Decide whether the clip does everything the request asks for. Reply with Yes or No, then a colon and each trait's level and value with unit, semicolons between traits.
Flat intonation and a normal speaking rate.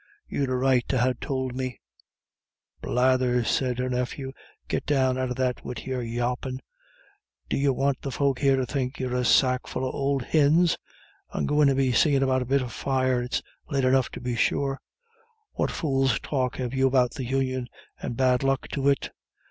Yes: narrow, 1.4 semitones; average, 195 wpm